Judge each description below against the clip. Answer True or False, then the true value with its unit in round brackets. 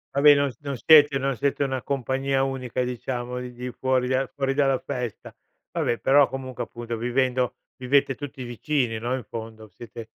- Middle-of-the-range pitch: False (130 Hz)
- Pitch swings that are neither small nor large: False (2.0 semitones)